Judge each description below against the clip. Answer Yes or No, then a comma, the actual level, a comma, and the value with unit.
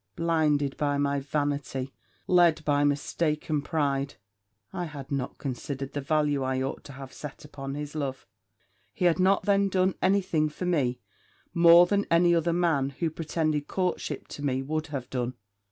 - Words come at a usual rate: Yes, average, 170 wpm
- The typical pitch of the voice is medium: Yes, medium, 150 Hz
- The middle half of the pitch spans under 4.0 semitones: Yes, average, 3.4 semitones